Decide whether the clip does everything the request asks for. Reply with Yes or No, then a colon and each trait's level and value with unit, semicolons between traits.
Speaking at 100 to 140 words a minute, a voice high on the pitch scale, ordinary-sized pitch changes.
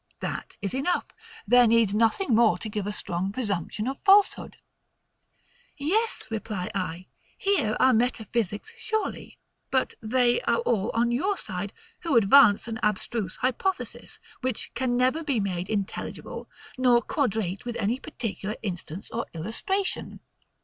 Yes: slow, 135 wpm; high, 230 Hz; average, 4.3 semitones